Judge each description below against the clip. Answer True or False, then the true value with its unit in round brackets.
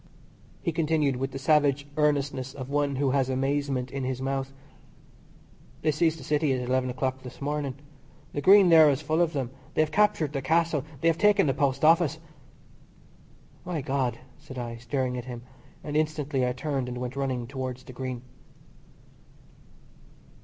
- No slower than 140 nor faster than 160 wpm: False (170 wpm)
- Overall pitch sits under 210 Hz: True (140 Hz)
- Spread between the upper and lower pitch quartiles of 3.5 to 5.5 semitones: False (2.9 semitones)